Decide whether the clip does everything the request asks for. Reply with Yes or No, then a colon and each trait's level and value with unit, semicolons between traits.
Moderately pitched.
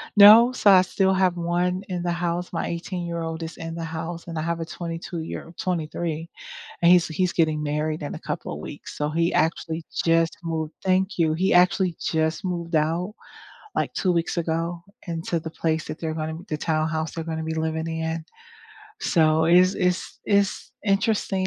Yes: medium, 165 Hz